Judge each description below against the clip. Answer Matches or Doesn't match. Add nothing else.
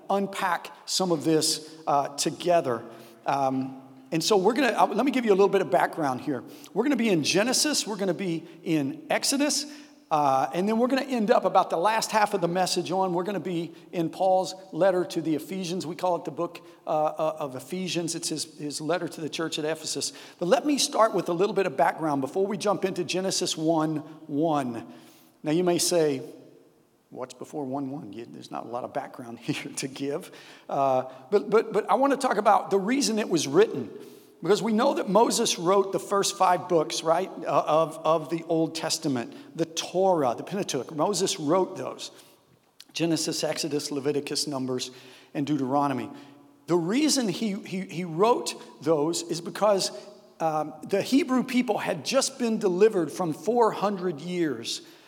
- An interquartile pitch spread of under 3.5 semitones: Doesn't match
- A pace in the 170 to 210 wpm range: Matches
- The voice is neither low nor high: Matches